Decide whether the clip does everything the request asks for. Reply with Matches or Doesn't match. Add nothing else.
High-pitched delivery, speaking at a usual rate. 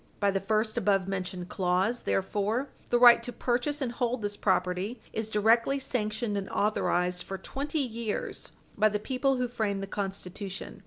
Matches